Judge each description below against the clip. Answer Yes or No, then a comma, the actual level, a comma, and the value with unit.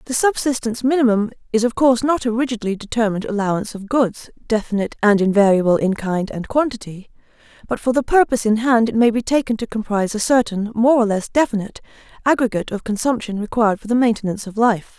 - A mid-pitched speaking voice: No, high, 225 Hz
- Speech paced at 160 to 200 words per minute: Yes, average, 190 wpm